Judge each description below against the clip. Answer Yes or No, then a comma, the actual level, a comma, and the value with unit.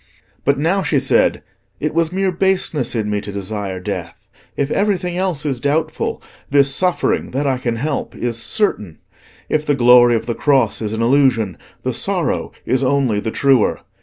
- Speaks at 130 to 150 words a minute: No, average, 175 wpm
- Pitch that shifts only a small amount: No, average, 5.3 semitones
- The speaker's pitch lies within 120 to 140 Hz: Yes, low, 135 Hz